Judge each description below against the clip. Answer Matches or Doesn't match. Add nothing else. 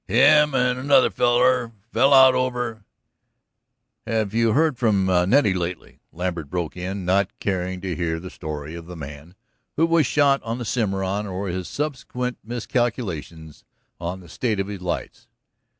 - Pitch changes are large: Matches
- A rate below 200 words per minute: Matches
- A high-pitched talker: Doesn't match